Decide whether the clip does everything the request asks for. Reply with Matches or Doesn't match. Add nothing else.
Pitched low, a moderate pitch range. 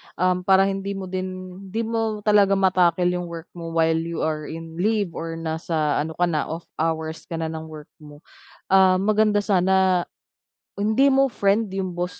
Doesn't match